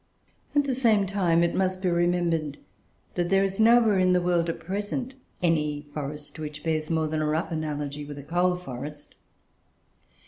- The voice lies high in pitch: No, medium, 170 Hz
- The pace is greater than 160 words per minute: Yes, average, 175 wpm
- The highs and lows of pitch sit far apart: No, average, 3.8 semitones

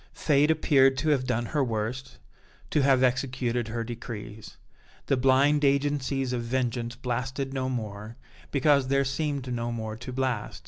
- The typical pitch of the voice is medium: No, low, 130 Hz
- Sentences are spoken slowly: No, average, 150 wpm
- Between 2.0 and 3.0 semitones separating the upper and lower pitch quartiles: Yes, narrow, 2.5 semitones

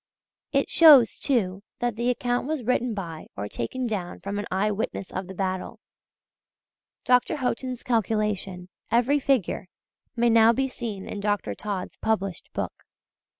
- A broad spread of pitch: No, average, 4.5 semitones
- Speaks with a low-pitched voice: No, high, 220 Hz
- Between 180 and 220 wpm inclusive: No, average, 150 wpm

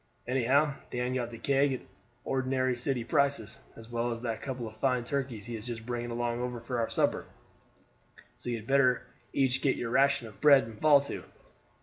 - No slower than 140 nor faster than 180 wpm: No, average, 195 wpm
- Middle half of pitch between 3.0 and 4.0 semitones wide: No, narrow, 2.4 semitones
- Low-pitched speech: Yes, low, 125 Hz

